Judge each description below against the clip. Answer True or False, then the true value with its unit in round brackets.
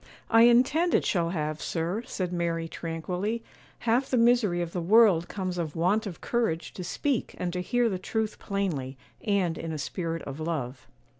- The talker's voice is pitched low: False (180 Hz)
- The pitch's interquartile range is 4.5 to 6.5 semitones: True (5.2 semitones)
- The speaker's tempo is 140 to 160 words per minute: False (180 wpm)